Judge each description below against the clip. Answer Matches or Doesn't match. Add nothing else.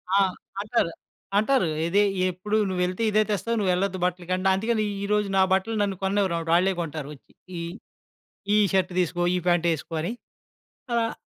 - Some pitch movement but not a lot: Matches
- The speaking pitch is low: Doesn't match